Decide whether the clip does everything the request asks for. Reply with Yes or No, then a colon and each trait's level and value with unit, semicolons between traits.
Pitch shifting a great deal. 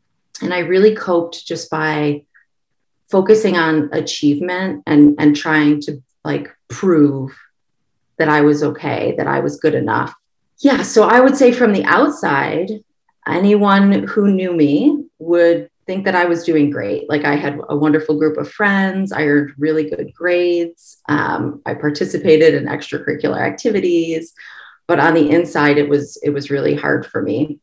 No: average, 4.2 semitones